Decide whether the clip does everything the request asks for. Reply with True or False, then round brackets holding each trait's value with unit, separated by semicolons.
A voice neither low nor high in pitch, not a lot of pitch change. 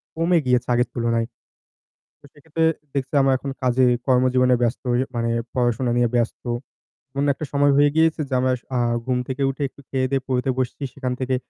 False (130 Hz; 2.0 semitones)